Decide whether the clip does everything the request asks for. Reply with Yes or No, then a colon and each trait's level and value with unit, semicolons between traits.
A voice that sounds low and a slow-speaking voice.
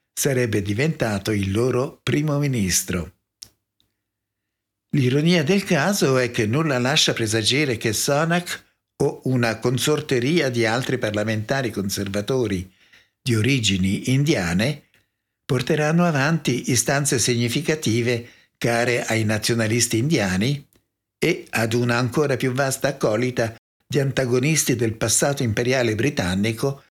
Yes: low, 125 Hz; slow, 105 wpm